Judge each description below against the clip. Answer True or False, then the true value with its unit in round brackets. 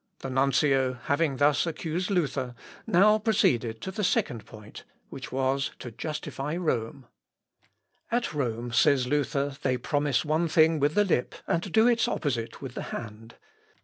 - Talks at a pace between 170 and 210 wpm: False (150 wpm)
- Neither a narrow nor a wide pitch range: True (4.7 semitones)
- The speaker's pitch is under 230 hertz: True (140 Hz)